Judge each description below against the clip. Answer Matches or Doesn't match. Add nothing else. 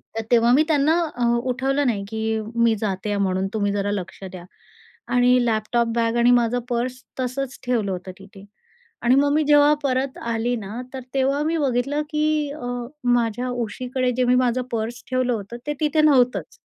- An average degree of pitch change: Matches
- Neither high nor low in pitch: Doesn't match